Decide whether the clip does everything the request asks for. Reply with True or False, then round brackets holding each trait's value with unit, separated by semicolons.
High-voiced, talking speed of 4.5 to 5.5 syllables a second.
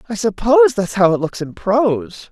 True (215 Hz; 5.2 syllables/s)